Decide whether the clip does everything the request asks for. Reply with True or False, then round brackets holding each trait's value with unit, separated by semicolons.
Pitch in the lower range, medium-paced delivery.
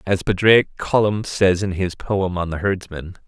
True (95 Hz; 185 wpm)